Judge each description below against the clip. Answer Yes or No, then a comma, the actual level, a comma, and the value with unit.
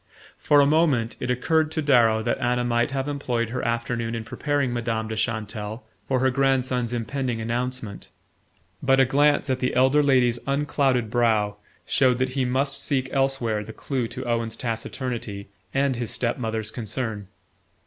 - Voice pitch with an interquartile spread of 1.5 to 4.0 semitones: Yes, average, 2.7 semitones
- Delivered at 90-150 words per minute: No, average, 165 wpm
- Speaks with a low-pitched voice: Yes, low, 125 Hz